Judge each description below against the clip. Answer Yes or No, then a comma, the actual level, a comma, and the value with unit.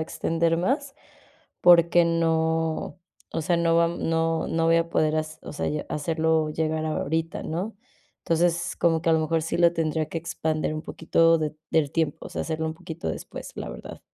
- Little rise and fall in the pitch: Yes, narrow, 1.0 semitones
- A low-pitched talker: No, medium, 165 Hz